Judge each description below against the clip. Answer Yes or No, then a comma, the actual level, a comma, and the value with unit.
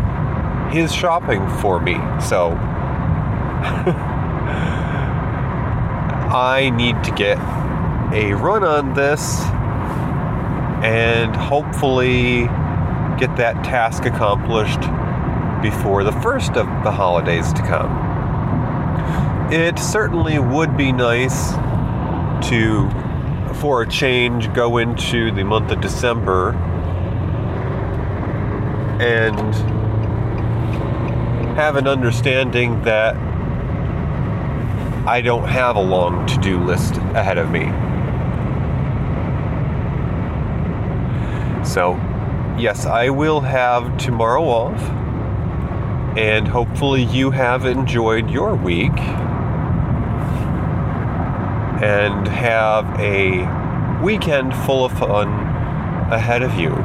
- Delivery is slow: Yes, slow, 85 wpm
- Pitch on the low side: Yes, low, 120 Hz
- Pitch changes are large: No, average, 3.4 semitones